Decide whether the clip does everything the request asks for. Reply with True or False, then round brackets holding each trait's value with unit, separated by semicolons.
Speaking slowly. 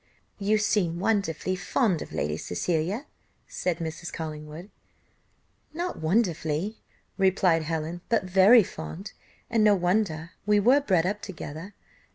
True (125 wpm)